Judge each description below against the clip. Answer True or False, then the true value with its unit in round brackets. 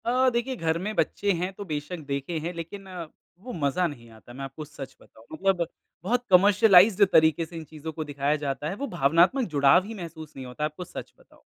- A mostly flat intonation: False (4.8 semitones)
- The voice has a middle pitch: True (165 Hz)